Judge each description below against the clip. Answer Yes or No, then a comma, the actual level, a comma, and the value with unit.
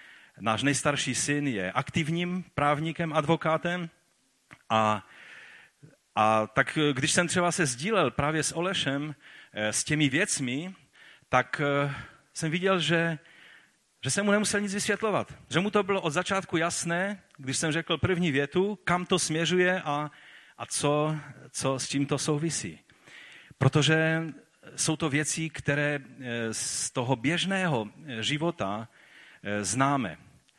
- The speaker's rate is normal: Yes, average, 125 wpm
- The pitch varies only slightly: No, average, 4.1 semitones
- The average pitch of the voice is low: No, medium, 150 Hz